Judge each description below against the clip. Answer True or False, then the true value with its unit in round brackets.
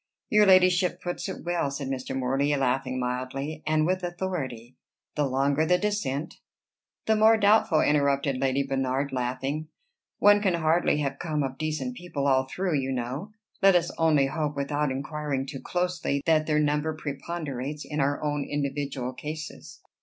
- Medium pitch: True (145 Hz)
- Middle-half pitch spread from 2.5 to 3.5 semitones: False (4.0 semitones)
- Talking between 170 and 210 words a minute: False (160 wpm)